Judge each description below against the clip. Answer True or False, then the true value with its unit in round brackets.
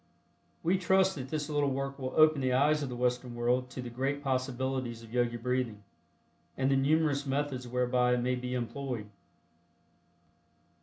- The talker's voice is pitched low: True (130 Hz)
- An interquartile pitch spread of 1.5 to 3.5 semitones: True (2.4 semitones)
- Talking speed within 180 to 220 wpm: False (165 wpm)